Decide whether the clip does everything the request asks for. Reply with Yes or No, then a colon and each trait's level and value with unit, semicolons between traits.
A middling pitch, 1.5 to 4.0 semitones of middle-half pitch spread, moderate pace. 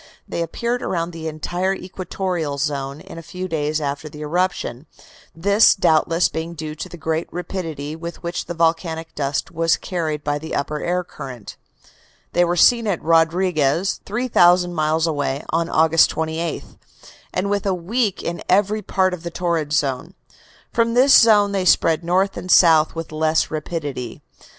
Yes: medium, 165 Hz; average, 2.9 semitones; average, 165 wpm